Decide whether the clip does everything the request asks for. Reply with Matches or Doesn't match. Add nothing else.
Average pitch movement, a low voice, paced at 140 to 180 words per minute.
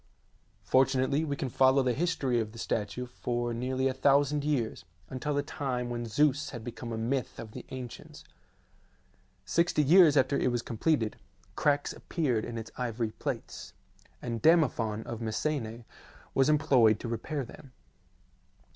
Matches